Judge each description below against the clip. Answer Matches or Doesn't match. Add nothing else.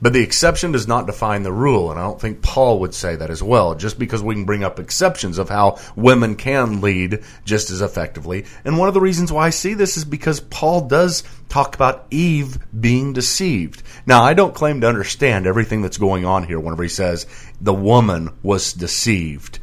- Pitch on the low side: Matches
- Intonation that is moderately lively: Doesn't match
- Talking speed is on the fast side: Matches